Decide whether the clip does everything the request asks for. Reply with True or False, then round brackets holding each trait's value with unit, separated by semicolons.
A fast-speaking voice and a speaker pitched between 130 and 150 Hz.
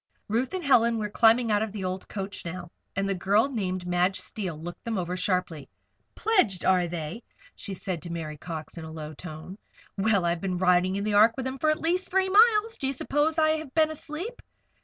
False (220 wpm; 200 Hz)